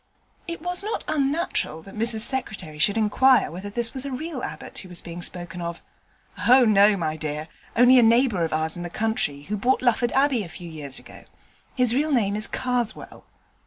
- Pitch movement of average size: No, wide, 6.7 semitones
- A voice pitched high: Yes, high, 220 Hz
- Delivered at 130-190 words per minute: No, average, 200 wpm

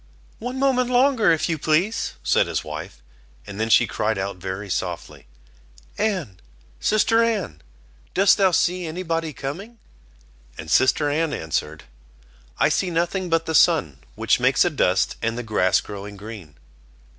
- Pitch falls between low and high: Yes, medium, 155 Hz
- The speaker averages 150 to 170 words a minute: Yes, average, 155 wpm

